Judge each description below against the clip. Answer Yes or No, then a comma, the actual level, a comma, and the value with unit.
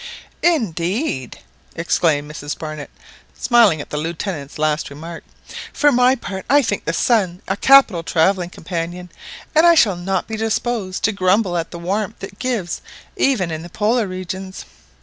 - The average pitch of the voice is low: No, medium, 185 Hz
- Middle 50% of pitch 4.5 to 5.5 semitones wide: Yes, average, 5.0 semitones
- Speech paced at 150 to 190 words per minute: Yes, average, 155 wpm